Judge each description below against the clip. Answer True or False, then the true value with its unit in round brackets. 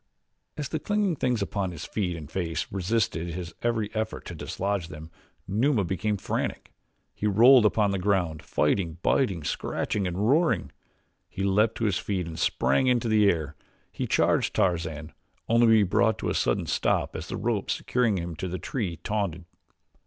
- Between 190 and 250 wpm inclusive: False (175 wpm)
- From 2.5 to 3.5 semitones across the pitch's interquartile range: False (4.5 semitones)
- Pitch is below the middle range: True (100 Hz)